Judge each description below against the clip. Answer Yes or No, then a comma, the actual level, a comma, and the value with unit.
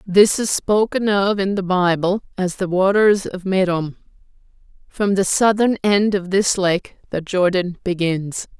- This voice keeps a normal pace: Yes, average, 155 wpm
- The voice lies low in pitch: No, high, 190 Hz